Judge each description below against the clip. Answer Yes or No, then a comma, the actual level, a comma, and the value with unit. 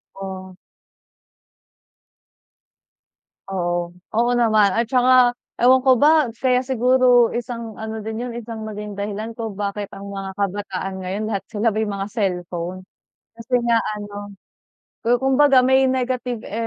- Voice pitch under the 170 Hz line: No, high, 220 Hz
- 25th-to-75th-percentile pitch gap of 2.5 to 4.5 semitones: Yes, average, 3.6 semitones